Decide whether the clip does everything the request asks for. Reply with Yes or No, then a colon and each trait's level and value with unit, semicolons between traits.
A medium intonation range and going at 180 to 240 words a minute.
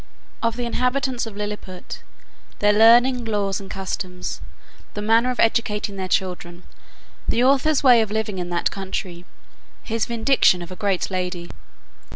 No: average, 4.1 semitones; average, 150 wpm